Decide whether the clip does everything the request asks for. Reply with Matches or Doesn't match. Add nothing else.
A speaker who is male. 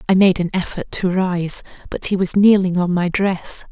Doesn't match